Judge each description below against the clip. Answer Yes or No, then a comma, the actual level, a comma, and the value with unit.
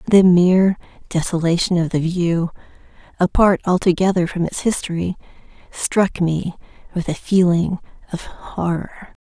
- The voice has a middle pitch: Yes, medium, 175 Hz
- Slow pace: Yes, slow, 115 wpm